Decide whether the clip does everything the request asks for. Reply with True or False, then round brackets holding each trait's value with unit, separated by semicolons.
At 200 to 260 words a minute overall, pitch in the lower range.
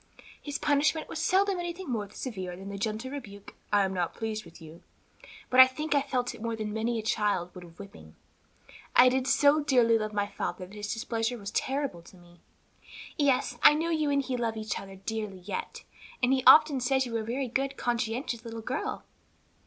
False (205 wpm; 230 Hz)